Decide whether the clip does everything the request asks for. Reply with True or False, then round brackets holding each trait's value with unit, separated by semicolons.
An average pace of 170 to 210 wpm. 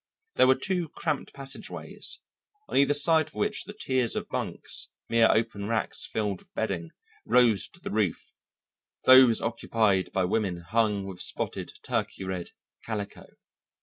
False (150 wpm)